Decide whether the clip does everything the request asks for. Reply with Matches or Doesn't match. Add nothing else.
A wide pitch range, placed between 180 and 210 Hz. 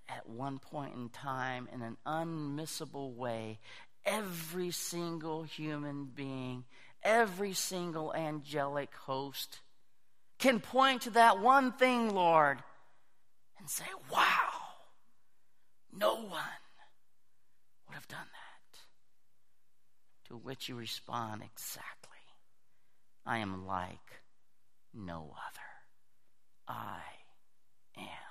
Doesn't match